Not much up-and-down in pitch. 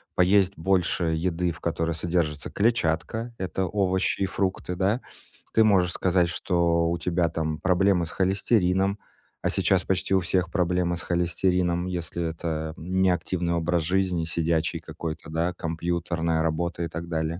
Yes: narrow, 2.0 semitones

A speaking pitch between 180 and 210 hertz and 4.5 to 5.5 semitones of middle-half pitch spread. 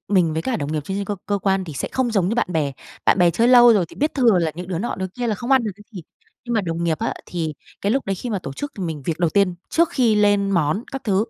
Yes: high, 195 Hz; average, 5.2 semitones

